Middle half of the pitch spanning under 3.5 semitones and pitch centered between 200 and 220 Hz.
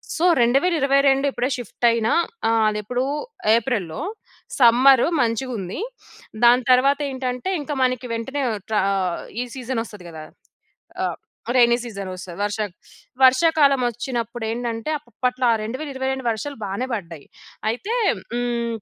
No: average, 3.0 semitones; high, 245 Hz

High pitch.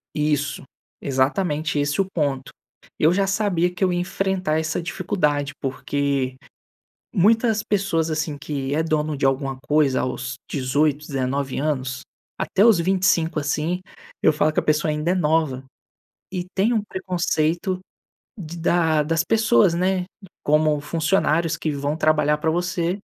No: medium, 155 Hz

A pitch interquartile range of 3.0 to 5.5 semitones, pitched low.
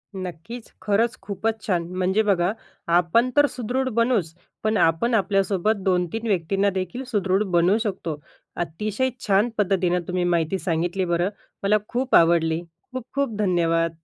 No: average, 4.1 semitones; high, 195 Hz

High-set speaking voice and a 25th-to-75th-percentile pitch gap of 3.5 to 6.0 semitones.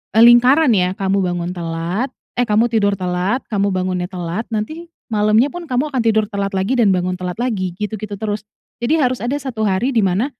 Yes: high, 210 Hz; average, 4.5 semitones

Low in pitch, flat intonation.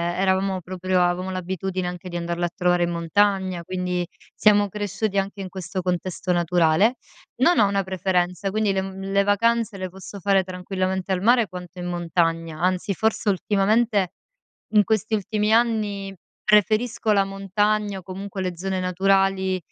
No: high, 190 Hz; narrow, 2.1 semitones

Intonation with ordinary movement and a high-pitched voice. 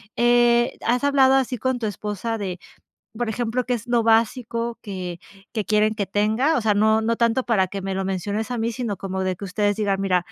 Yes: average, 3.3 semitones; high, 220 Hz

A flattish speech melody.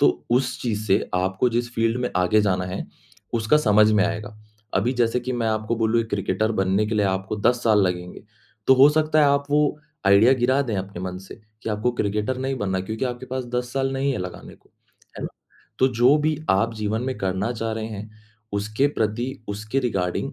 No: average, 3.5 semitones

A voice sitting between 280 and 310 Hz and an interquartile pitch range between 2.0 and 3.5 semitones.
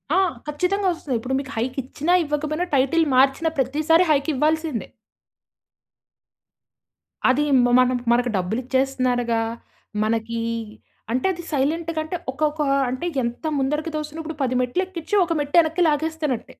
No: very high, 290 Hz; average, 3.9 semitones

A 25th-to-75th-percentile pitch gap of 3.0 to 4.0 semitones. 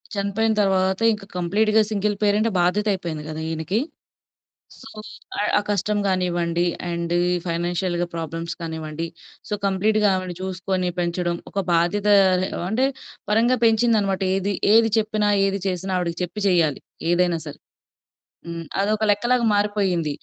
Yes: average, 3.4 semitones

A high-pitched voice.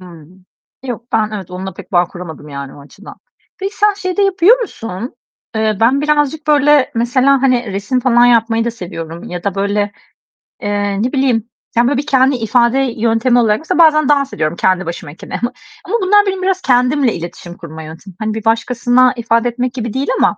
Yes: high, 235 Hz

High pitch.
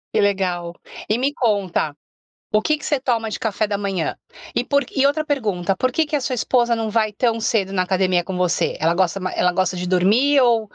Yes: high, 210 Hz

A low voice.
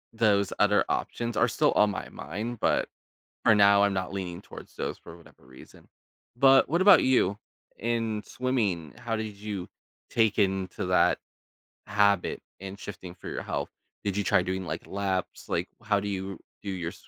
Yes: low, 100 Hz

